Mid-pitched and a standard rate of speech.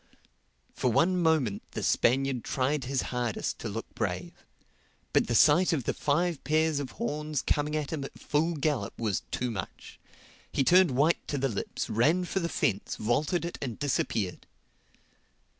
Yes: medium, 145 Hz; average, 165 wpm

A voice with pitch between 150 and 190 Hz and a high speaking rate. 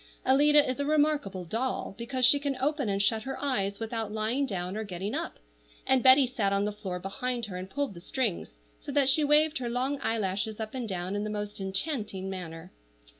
No: high, 225 Hz; fast, 210 wpm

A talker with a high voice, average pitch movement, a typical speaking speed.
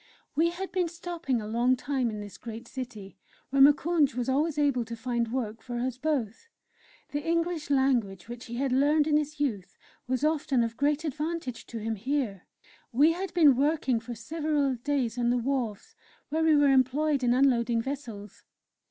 Yes: very high, 265 Hz; average, 4.1 semitones; average, 180 wpm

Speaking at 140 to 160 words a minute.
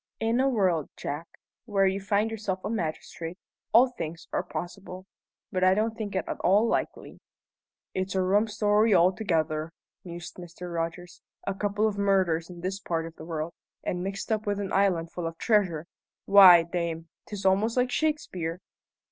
No: average, 175 wpm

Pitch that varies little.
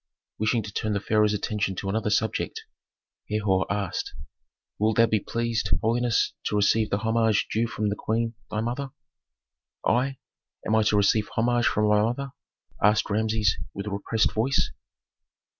Yes: narrow, 1.8 semitones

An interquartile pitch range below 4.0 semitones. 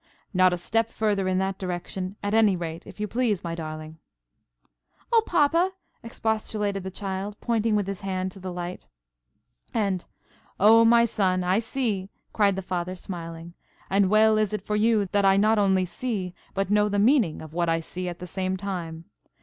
Yes: average, 2.9 semitones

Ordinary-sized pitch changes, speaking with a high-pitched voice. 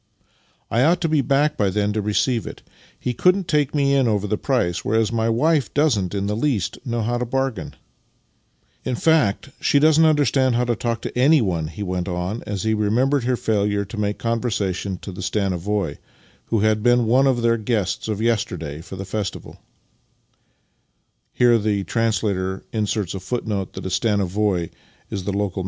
No: average, 4.6 semitones; low, 115 Hz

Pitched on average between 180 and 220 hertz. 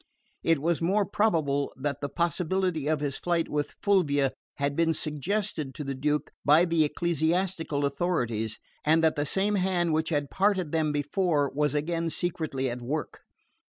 No: medium, 155 Hz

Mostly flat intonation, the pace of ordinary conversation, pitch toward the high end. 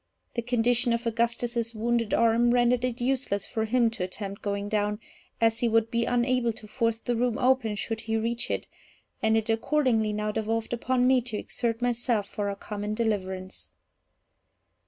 Yes: narrow, 2.1 semitones; average, 175 wpm; high, 230 Hz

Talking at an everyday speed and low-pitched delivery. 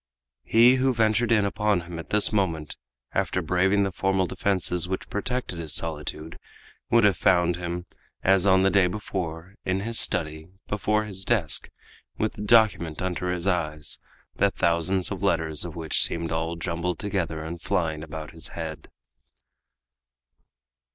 Yes: average, 155 wpm; very low, 90 Hz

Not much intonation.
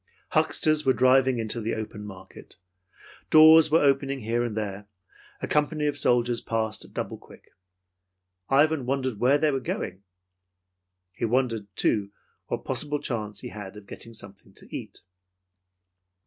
No: average, 4.7 semitones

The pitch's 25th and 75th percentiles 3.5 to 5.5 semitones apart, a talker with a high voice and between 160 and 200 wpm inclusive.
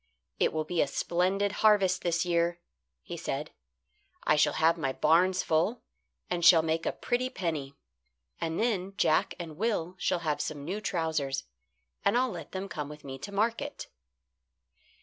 No: average, 3.9 semitones; medium, 170 Hz; average, 165 wpm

